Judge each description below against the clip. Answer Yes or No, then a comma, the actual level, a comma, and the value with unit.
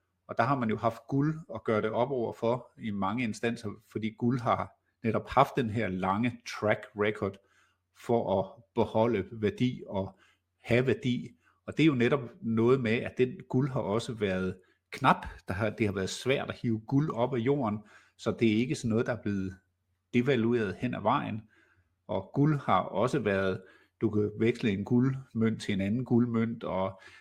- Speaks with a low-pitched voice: Yes, low, 115 Hz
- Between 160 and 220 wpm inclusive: Yes, average, 190 wpm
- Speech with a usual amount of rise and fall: Yes, average, 3.3 semitones